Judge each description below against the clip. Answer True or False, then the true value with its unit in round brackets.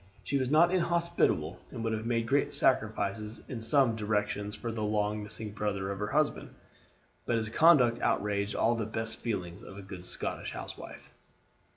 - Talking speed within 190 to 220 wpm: False (175 wpm)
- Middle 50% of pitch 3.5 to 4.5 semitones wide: False (2.6 semitones)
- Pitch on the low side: True (110 Hz)